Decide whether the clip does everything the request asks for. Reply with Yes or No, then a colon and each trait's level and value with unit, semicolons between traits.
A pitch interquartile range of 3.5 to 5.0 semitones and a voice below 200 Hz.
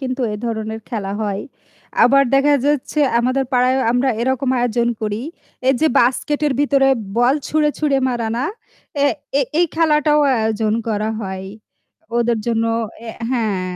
No: average, 3.8 semitones; high, 245 Hz